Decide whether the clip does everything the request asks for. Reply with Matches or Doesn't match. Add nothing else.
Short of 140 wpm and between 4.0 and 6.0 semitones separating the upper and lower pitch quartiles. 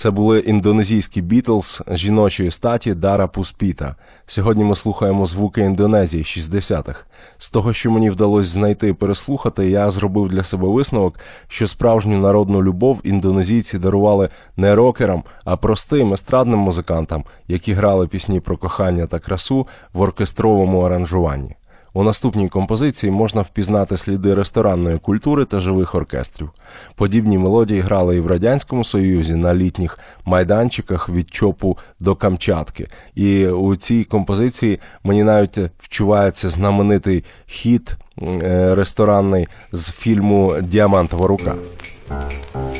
Doesn't match